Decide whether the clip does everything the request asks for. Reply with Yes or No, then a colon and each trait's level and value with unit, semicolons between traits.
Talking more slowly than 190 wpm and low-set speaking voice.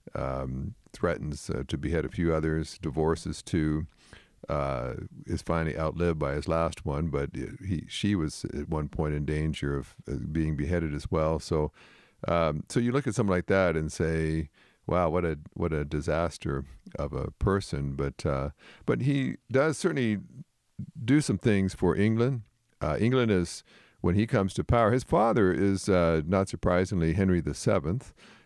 Yes: average, 170 wpm; very low, 85 Hz